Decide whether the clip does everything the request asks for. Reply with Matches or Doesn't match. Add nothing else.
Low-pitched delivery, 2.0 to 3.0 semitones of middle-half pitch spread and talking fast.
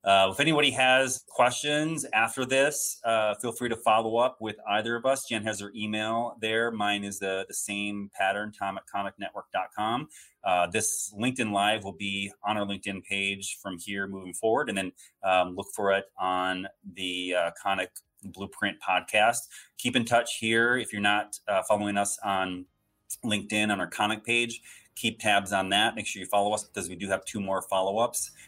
Doesn't match